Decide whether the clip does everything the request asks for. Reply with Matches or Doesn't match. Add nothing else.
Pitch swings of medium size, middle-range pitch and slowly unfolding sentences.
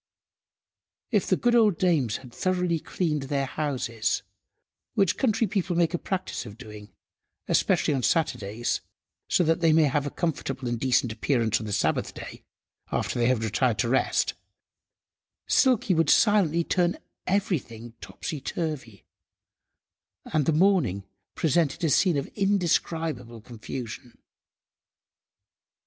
Doesn't match